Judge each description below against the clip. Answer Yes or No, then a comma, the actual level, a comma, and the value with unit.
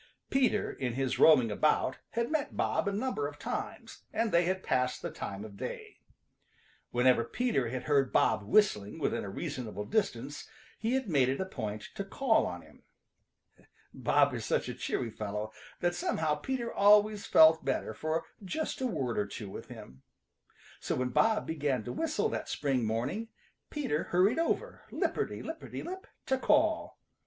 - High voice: No, medium, 155 Hz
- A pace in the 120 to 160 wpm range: No, average, 170 wpm